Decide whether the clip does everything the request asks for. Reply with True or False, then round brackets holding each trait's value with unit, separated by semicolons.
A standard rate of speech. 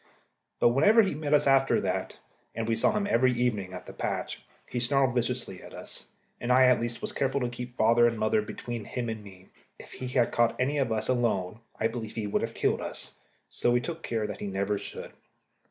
False (230 wpm)